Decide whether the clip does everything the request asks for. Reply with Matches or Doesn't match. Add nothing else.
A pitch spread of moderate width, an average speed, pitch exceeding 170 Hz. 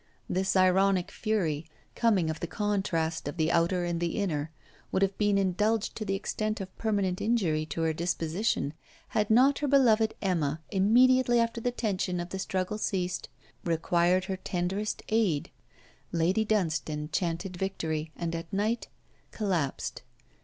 Matches